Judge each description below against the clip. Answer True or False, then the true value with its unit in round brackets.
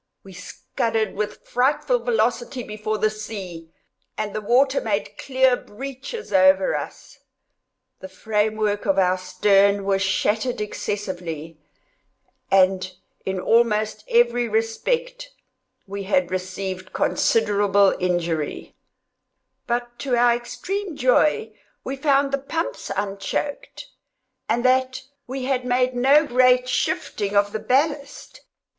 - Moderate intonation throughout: True (4.6 semitones)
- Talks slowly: True (115 wpm)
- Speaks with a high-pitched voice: True (220 Hz)